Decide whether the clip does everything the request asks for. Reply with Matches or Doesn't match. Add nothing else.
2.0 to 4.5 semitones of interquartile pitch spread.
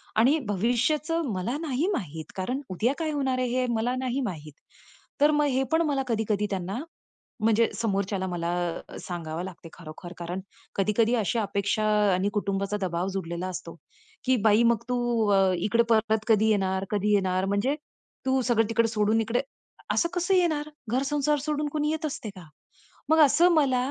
Doesn't match